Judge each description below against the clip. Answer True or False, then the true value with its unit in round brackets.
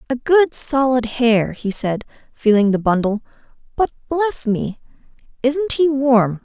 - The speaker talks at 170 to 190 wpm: False (140 wpm)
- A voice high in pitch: True (240 Hz)